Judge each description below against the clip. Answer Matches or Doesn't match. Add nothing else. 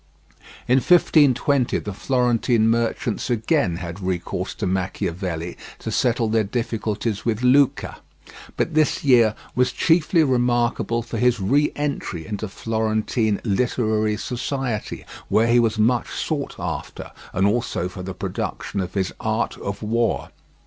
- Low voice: Matches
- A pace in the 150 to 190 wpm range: Doesn't match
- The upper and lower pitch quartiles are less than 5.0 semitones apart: Matches